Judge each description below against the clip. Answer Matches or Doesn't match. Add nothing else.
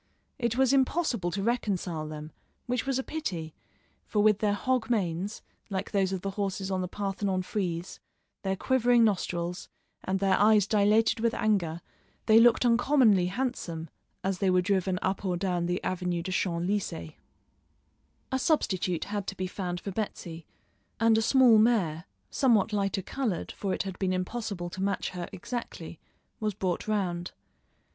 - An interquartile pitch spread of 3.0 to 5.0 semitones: Matches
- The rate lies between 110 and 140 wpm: Doesn't match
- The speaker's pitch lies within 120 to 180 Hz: Doesn't match